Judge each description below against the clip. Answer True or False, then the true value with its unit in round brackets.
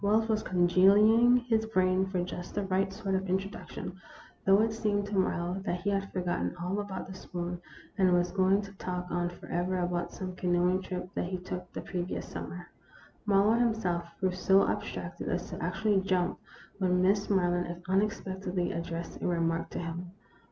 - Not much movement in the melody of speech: True (2.1 semitones)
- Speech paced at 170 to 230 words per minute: True (180 wpm)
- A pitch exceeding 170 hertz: True (185 Hz)